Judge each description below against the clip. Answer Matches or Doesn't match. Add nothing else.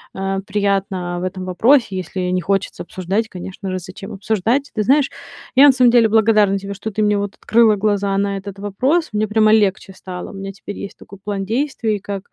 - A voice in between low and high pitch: Doesn't match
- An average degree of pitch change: Doesn't match